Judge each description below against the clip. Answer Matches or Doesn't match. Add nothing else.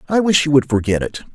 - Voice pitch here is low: Doesn't match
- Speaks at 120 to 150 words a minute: Doesn't match